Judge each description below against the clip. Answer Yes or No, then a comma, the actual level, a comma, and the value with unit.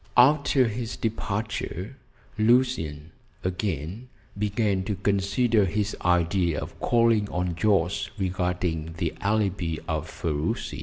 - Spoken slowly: Yes, slow, 105 wpm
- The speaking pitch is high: No, low, 100 Hz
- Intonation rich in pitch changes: No, average, 4.1 semitones